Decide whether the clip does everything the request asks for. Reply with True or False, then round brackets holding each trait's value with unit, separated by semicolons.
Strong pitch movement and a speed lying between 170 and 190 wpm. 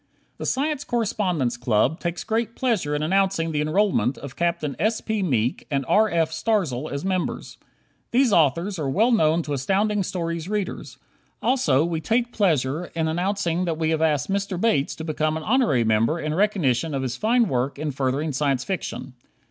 True (5.9 semitones; 180 wpm)